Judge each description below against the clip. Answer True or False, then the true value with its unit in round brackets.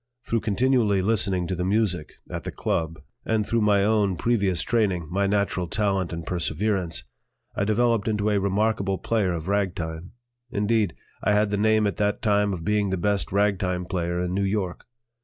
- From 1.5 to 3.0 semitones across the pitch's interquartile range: True (2.6 semitones)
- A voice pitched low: True (100 Hz)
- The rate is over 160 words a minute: True (175 wpm)